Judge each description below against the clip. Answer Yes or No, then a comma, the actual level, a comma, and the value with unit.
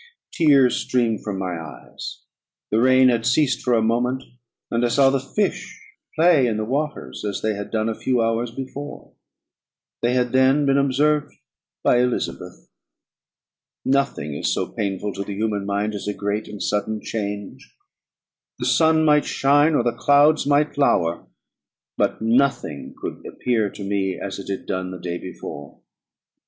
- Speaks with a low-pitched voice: Yes, low, 120 Hz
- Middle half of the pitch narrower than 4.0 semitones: No, average, 5.1 semitones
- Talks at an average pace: Yes, average, 165 wpm